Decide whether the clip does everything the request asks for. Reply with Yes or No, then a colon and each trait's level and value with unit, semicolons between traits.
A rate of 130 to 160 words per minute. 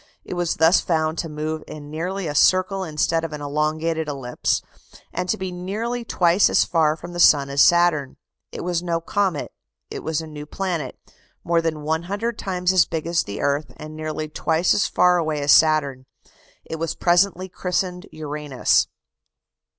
No: average, 175 wpm